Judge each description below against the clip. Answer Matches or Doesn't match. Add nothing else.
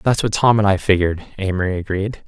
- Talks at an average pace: Doesn't match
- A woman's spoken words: Doesn't match